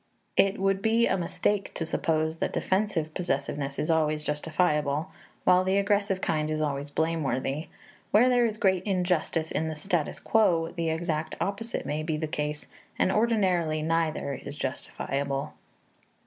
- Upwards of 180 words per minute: No, average, 150 wpm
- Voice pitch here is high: No, medium, 165 Hz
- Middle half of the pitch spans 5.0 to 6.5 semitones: No, average, 4.0 semitones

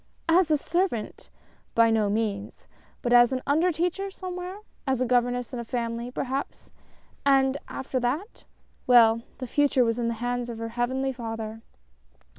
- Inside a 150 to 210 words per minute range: Yes, average, 170 wpm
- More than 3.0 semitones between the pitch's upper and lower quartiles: Yes, average, 3.4 semitones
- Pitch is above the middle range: Yes, high, 245 Hz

